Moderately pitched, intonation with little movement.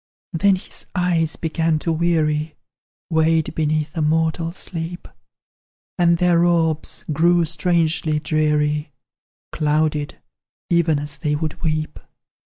Yes: medium, 160 Hz; narrow, 1.8 semitones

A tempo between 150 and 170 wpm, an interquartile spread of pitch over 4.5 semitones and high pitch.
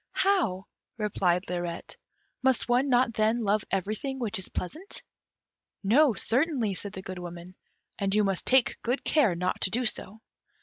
Yes: average, 160 wpm; average, 5.0 semitones; high, 215 Hz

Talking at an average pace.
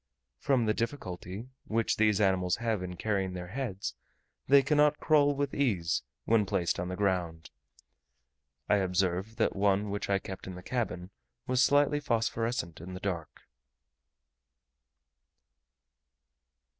No: slow, 130 wpm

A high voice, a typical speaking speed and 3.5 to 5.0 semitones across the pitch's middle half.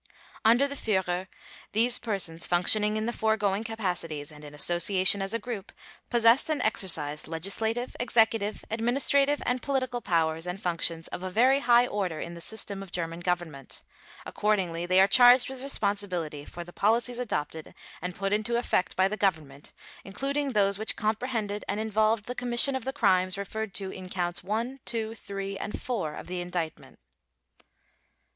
Yes: high, 200 Hz; average, 165 wpm; average, 4.7 semitones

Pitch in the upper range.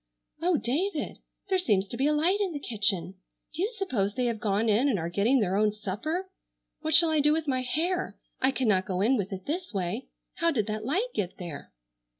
Yes: very high, 250 Hz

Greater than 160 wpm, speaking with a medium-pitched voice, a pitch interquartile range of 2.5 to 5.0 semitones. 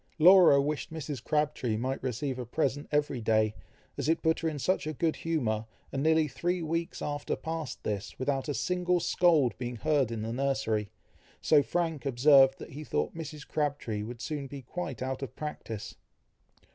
Yes: average, 175 wpm; medium, 145 Hz; average, 4.2 semitones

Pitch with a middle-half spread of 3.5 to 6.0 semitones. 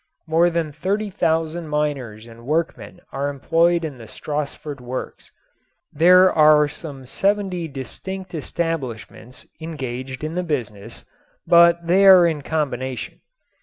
Yes: average, 4.5 semitones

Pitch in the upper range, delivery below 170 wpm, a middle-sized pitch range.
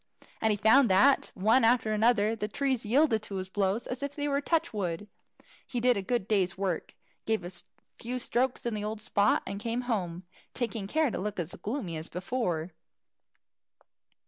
No: high, 220 Hz; average, 185 wpm; average, 4.2 semitones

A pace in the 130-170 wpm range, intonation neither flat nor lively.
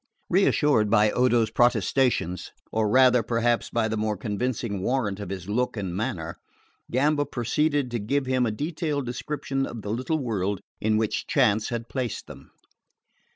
Yes: average, 155 wpm; average, 3.7 semitones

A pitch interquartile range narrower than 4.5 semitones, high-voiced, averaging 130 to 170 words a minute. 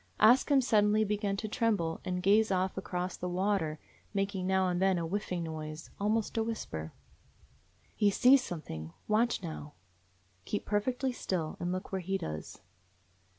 Yes: average, 3.4 semitones; high, 195 Hz; average, 160 wpm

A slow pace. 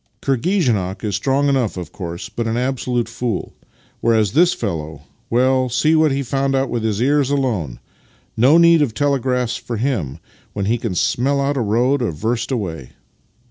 No: average, 180 wpm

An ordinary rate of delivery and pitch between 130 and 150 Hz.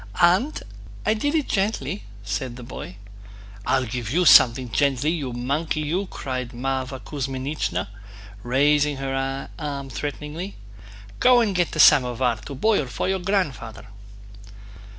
No: slow, 130 wpm; medium, 140 Hz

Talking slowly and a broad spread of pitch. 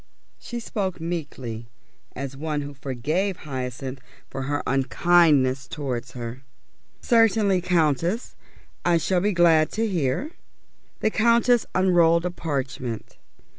Yes: slow, 120 wpm; wide, 5.8 semitones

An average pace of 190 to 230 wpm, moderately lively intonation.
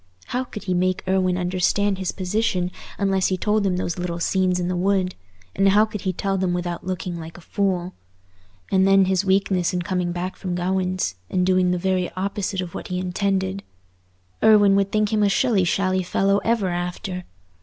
No: average, 195 wpm; narrow, 1.6 semitones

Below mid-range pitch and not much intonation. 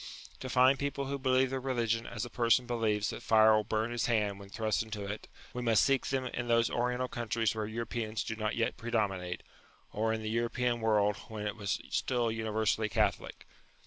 Yes: low, 115 Hz; narrow, 2.2 semitones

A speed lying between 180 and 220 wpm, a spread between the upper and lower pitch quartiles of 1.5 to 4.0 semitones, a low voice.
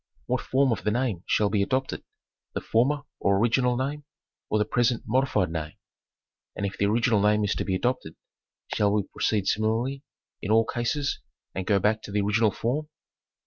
Yes: average, 185 wpm; average, 3.7 semitones; low, 110 Hz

